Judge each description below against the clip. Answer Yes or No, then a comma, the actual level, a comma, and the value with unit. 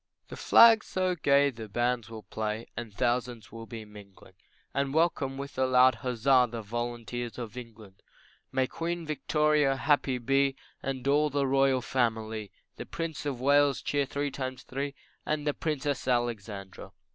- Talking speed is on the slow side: No, average, 155 wpm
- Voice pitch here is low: Yes, low, 130 Hz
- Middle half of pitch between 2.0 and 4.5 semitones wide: Yes, average, 3.5 semitones